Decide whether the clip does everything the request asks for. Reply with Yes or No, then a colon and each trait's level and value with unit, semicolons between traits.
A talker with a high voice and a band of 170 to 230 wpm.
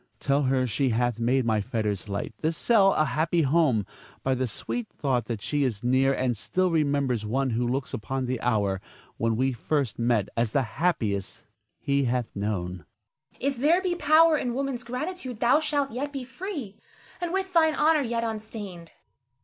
No: medium, 140 Hz; average, 180 wpm